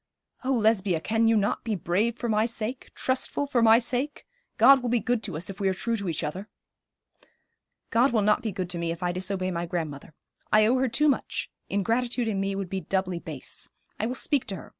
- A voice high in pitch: Yes, high, 215 Hz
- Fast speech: Yes, fast, 225 wpm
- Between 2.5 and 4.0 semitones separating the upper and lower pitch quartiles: No, average, 4.4 semitones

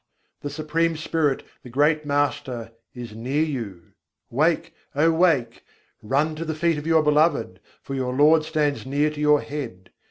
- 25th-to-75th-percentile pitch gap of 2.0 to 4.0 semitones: Yes, average, 3.2 semitones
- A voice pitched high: No, medium, 150 Hz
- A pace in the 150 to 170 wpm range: Yes, average, 160 wpm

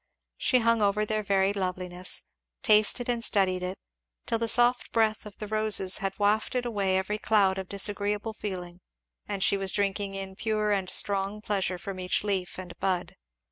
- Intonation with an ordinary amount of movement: No, narrow, 2.1 semitones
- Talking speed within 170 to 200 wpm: Yes, average, 175 wpm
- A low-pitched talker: No, high, 200 Hz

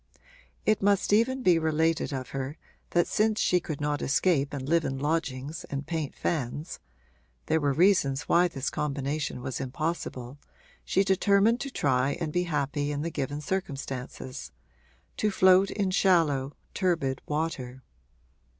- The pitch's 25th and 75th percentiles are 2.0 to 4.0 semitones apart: No, average, 4.7 semitones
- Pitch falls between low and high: Yes, medium, 150 Hz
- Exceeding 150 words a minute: No, average, 145 wpm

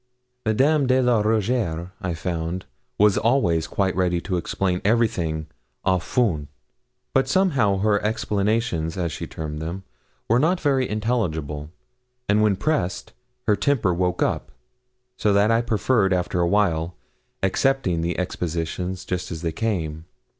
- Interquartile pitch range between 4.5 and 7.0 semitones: Yes, average, 4.9 semitones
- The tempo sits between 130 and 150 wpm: Yes, average, 140 wpm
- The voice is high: No, very low, 95 Hz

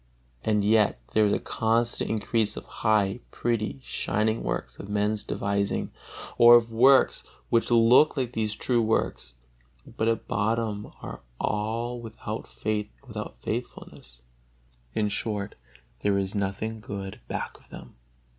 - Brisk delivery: No, average, 140 wpm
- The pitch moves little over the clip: Yes, narrow, 2.0 semitones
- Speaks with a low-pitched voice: Yes, low, 110 Hz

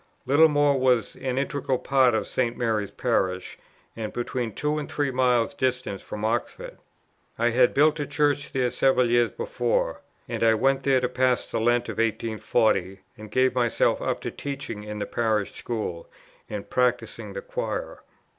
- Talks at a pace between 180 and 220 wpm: No, average, 165 wpm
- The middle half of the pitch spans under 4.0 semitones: Yes, average, 3.4 semitones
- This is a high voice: No, low, 125 Hz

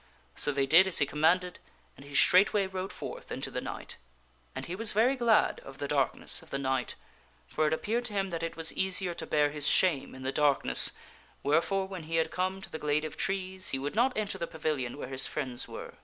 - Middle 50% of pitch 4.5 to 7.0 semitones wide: Yes, average, 4.9 semitones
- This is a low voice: No, medium, 165 Hz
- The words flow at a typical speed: No, fast, 230 wpm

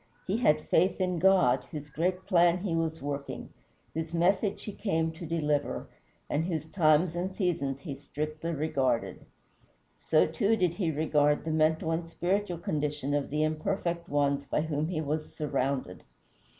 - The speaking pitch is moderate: Yes, medium, 160 Hz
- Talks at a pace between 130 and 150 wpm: No, average, 160 wpm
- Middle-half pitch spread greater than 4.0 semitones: No, average, 3.0 semitones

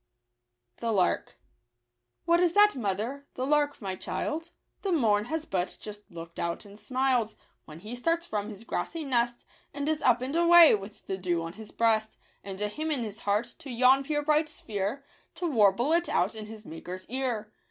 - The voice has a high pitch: Yes, high, 235 Hz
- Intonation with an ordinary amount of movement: No, wide, 6.2 semitones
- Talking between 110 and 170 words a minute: No, average, 195 wpm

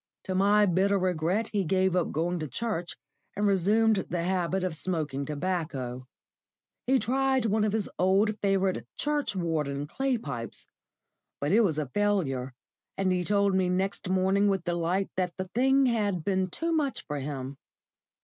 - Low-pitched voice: No, medium, 185 Hz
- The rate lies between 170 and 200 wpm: No, average, 160 wpm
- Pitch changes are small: No, average, 3.8 semitones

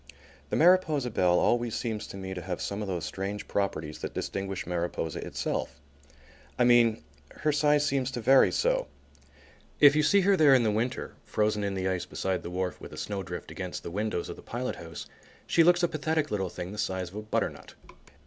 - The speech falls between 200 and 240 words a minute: Yes, fast, 205 wpm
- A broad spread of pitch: Yes, wide, 7.1 semitones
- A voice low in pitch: Yes, low, 105 Hz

